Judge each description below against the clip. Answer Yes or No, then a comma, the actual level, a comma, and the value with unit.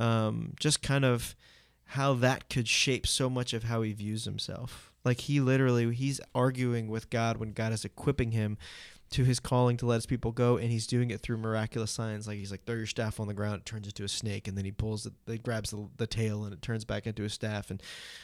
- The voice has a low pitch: Yes, low, 115 Hz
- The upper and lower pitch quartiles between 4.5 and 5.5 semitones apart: No, narrow, 2.6 semitones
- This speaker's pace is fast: Yes, fast, 245 wpm